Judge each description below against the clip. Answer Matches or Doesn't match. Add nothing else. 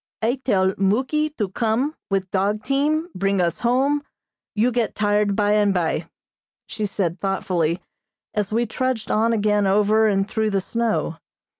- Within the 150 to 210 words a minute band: Matches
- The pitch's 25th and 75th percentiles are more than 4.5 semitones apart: Doesn't match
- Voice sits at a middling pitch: Doesn't match